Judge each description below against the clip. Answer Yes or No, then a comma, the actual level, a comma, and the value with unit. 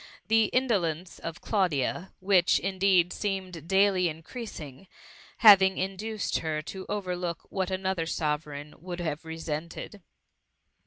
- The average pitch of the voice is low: No, medium, 185 Hz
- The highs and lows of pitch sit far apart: No, average, 3.2 semitones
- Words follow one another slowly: Yes, slow, 120 wpm